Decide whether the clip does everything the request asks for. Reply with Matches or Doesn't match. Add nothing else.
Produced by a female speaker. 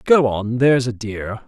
Doesn't match